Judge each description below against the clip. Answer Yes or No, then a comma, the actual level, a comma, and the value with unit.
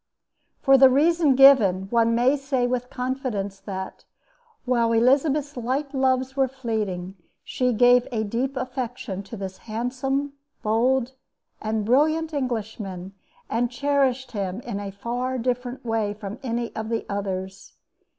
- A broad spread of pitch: No, average, 3.6 semitones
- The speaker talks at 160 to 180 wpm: No, slow, 135 wpm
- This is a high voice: Yes, high, 245 Hz